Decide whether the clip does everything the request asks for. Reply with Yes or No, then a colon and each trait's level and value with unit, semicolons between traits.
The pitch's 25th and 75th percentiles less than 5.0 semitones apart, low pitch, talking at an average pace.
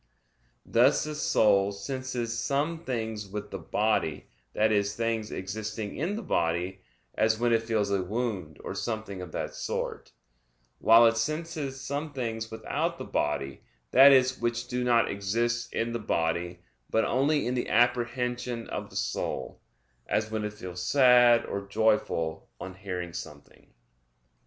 Yes: average, 3.7 semitones; low, 115 Hz; average, 150 wpm